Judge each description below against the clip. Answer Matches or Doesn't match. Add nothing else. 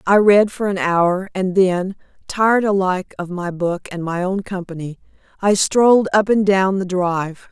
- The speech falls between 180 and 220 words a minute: Matches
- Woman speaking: Matches